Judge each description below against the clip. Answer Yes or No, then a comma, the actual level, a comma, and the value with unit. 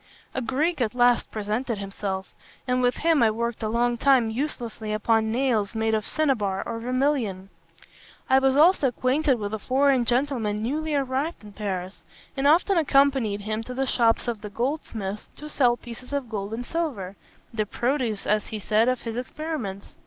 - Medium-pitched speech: No, high, 240 Hz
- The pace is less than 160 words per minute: No, average, 175 wpm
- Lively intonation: No, average, 4.0 semitones